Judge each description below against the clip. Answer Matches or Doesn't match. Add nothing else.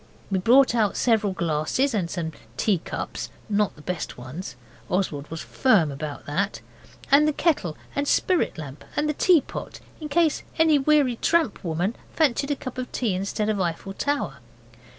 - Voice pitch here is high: Matches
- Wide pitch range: Matches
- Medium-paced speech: Matches